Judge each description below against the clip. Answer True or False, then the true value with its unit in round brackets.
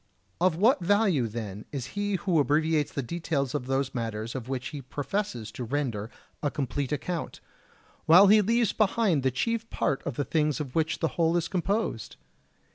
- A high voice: False (150 Hz)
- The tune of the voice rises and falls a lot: True (5.9 semitones)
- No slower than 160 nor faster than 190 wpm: True (180 wpm)